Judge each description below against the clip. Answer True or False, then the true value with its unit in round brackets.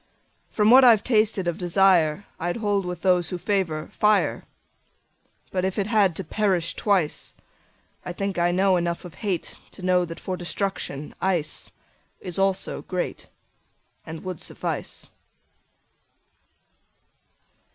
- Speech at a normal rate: False (110 wpm)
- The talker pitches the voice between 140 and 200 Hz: True (185 Hz)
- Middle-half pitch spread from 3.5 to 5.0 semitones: False (2.4 semitones)